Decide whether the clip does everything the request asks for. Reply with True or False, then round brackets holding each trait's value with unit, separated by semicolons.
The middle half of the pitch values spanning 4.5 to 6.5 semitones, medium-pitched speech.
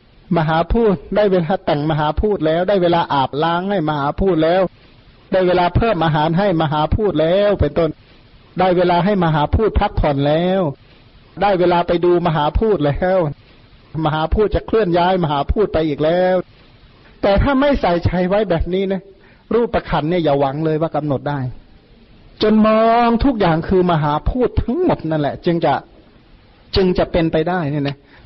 False (4.1 semitones; 170 Hz)